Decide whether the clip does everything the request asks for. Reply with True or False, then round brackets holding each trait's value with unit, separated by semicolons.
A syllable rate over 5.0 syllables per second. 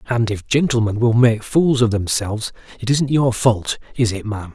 True (5.2 syllables/s)